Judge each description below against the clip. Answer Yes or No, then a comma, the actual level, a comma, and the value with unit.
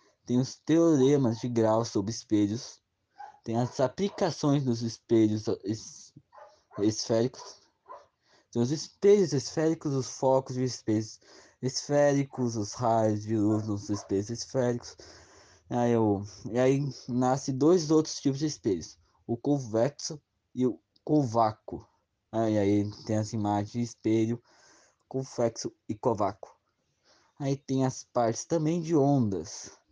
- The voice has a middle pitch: No, low, 120 Hz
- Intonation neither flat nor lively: Yes, average, 4.0 semitones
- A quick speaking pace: No, average, 125 wpm